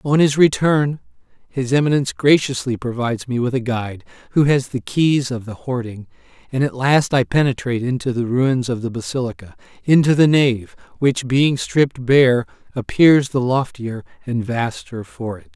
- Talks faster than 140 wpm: Yes, average, 165 wpm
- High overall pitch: No, low, 130 Hz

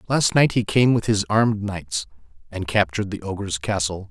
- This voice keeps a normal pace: Yes, average, 190 wpm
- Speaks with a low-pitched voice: Yes, low, 100 Hz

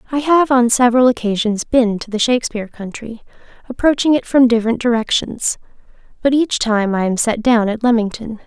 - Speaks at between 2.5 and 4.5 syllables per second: No, 5.6 syllables/s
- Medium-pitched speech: No, high, 235 Hz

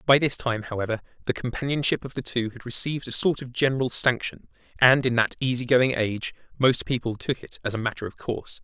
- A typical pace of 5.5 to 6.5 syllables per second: Yes, 6.1 syllables/s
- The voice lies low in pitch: Yes, low, 125 Hz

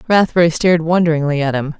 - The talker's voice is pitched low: No, medium, 160 Hz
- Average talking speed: Yes, average, 165 wpm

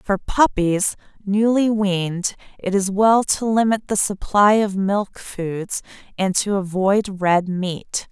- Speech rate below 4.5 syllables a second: Yes, 3.5 syllables/s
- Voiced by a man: No, female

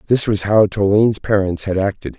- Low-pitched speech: Yes, low, 100 Hz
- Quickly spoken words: No, average, 190 wpm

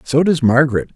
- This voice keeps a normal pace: Yes, average, 190 wpm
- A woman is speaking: No, male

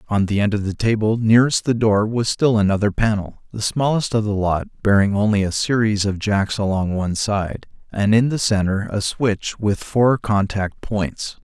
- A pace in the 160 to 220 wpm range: Yes, average, 195 wpm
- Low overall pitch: Yes, low, 105 Hz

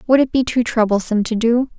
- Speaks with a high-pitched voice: Yes, high, 235 Hz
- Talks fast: Yes, fast, 235 wpm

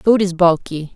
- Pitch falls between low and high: Yes, medium, 180 Hz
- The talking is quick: No, average, 190 wpm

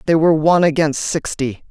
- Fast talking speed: No, average, 175 wpm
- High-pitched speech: No, medium, 160 Hz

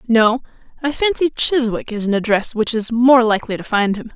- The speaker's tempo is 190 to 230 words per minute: Yes, average, 200 wpm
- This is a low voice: No, high, 235 Hz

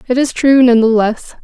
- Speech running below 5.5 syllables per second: Yes, 4.8 syllables/s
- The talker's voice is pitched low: No, high, 245 Hz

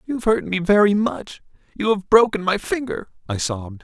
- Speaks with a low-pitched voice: No, high, 190 Hz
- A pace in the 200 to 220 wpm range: No, average, 170 wpm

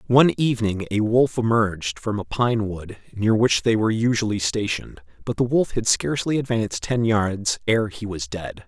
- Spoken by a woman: No, male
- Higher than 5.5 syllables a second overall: No, 5.1 syllables/s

